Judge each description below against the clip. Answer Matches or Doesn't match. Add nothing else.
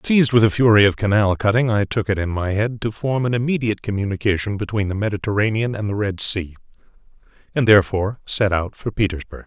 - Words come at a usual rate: Matches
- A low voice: Matches